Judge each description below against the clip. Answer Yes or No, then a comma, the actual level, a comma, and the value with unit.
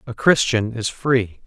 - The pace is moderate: Yes, average, 165 wpm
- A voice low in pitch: Yes, low, 115 Hz